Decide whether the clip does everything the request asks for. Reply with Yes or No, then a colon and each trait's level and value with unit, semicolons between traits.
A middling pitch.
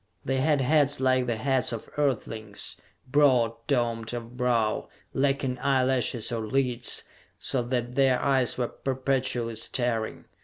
No: low, 125 Hz